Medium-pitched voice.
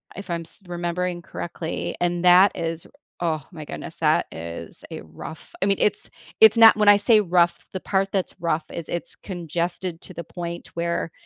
Yes: medium, 175 Hz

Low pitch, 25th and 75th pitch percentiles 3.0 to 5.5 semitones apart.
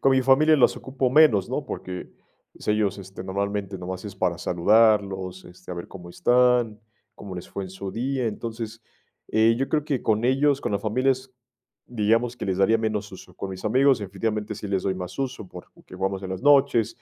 Yes: low, 105 Hz; average, 4.6 semitones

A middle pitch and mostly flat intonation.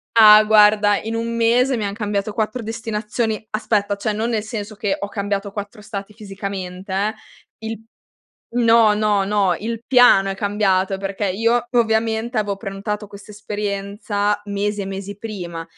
No: high, 210 Hz; narrow, 1.8 semitones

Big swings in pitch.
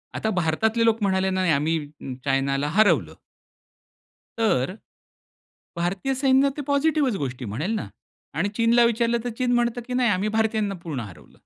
Yes: wide, 7.1 semitones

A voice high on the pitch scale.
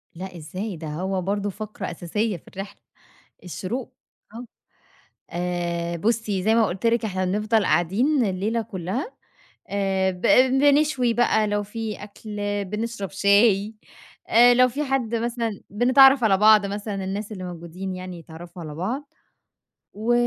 Yes: high, 205 Hz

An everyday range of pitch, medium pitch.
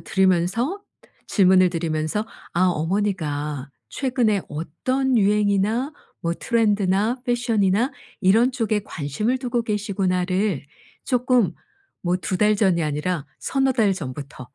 No: average, 5.0 semitones; high, 200 Hz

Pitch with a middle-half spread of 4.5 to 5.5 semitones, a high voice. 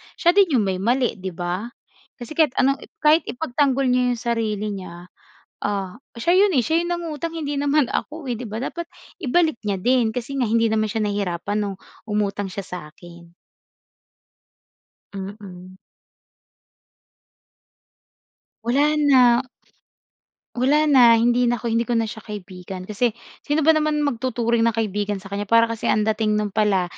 Yes: average, 5.1 semitones; high, 230 Hz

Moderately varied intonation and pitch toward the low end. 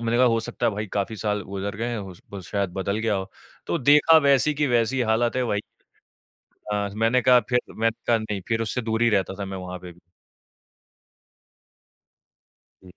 Yes: average, 3.2 semitones; low, 110 Hz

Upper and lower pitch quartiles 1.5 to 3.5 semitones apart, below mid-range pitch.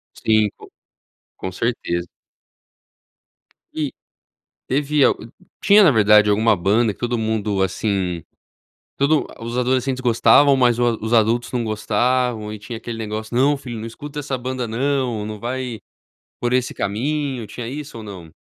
Yes: average, 3.2 semitones; low, 120 Hz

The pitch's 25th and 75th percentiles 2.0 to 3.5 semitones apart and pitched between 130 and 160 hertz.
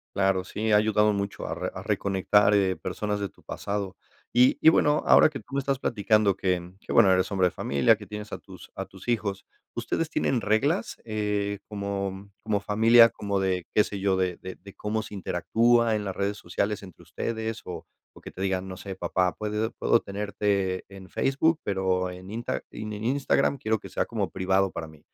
No: narrow, 2.5 semitones; low, 100 Hz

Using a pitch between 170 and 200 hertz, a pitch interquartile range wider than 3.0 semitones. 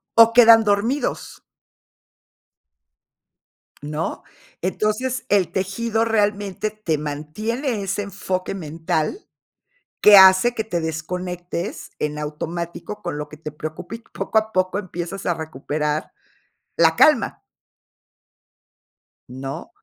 Yes: medium, 185 Hz; average, 5.3 semitones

